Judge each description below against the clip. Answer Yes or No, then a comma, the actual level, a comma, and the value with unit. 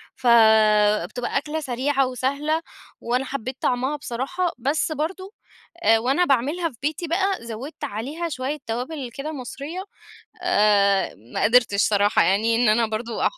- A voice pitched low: No, very high, 255 Hz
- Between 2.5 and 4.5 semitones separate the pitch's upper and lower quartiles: No, average, 5.1 semitones